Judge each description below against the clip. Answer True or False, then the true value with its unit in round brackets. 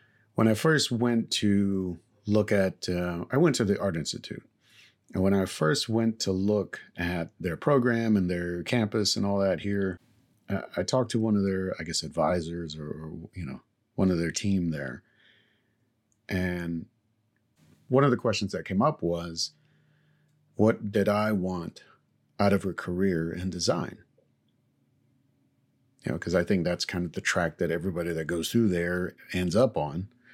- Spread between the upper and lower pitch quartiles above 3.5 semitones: True (4.2 semitones)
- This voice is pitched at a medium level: False (100 Hz)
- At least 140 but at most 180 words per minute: True (170 wpm)